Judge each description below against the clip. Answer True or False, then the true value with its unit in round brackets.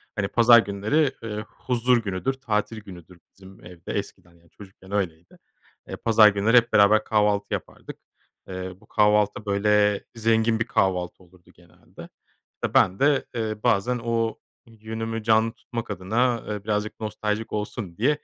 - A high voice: False (105 Hz)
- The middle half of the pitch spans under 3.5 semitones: True (2.7 semitones)